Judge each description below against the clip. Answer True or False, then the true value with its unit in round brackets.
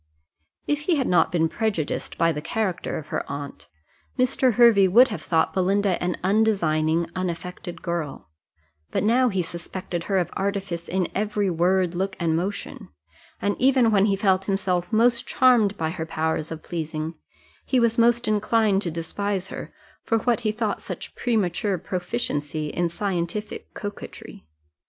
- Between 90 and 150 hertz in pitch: False (190 Hz)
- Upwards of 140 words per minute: True (155 wpm)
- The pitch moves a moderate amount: True (4.3 semitones)